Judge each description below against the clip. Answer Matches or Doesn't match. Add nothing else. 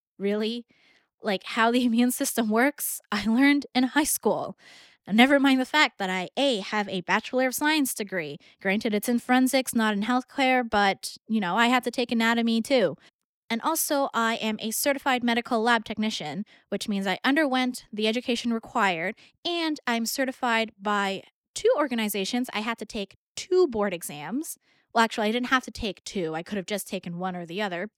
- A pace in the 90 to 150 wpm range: Doesn't match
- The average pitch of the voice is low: Doesn't match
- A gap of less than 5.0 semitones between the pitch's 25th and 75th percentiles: Matches